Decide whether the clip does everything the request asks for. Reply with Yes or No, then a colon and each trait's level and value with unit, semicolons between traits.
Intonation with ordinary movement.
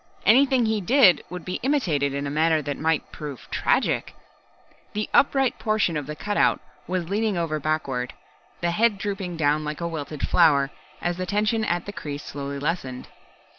No: wide, 5.8 semitones